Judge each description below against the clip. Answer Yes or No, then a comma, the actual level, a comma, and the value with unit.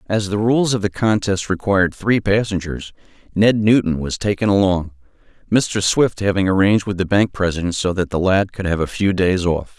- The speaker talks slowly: No, average, 195 wpm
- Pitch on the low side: Yes, very low, 95 Hz